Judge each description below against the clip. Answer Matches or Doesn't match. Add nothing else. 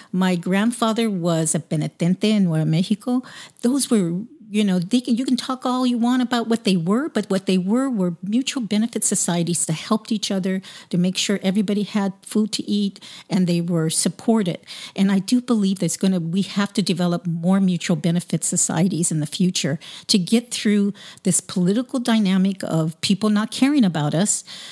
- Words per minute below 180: Doesn't match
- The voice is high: Matches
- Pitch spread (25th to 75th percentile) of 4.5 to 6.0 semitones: Doesn't match